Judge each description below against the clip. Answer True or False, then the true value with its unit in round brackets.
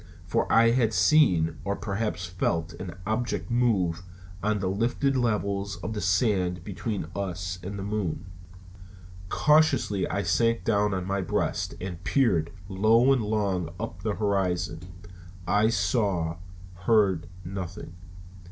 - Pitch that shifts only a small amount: False (3.6 semitones)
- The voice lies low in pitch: True (100 Hz)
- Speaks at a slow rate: True (130 wpm)